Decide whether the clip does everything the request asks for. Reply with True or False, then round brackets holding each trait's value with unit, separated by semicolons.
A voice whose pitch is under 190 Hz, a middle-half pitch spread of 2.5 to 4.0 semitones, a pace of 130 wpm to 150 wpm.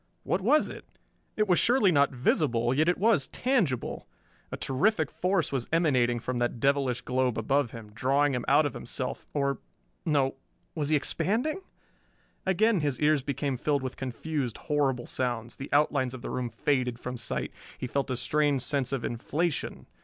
False (140 Hz; 3.7 semitones; 170 wpm)